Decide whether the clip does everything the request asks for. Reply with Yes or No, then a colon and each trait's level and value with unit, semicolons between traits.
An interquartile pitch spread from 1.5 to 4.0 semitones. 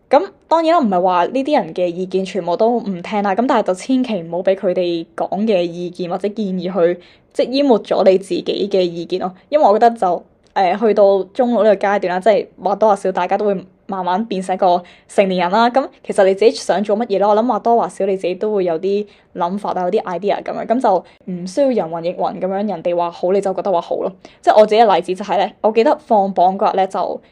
Yes: average, 3.2 semitones